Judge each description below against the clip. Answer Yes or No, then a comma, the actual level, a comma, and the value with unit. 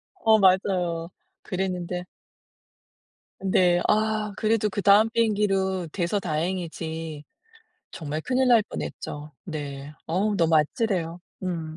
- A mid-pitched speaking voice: Yes, medium, 180 Hz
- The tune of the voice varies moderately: Yes, average, 4.2 semitones